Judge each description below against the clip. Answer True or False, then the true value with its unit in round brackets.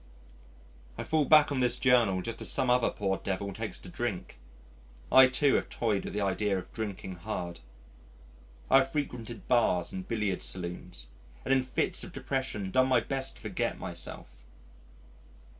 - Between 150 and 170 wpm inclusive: True (165 wpm)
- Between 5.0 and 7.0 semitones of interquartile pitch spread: True (5.5 semitones)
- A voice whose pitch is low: True (115 Hz)